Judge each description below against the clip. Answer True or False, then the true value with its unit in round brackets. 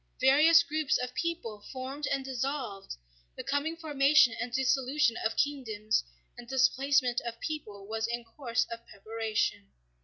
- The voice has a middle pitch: False (260 Hz)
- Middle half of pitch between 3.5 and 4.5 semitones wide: True (4.0 semitones)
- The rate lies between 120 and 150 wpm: True (140 wpm)